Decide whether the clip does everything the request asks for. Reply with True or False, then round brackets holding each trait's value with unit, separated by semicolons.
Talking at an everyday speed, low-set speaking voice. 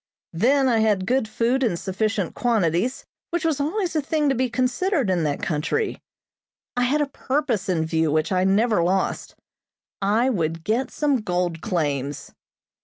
False (165 wpm; 220 Hz)